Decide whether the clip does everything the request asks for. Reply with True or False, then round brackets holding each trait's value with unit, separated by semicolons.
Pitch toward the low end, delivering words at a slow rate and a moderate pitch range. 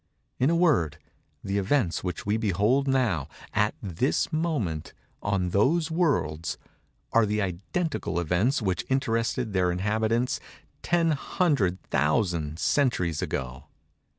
False (105 Hz; 105 wpm; 7.3 semitones)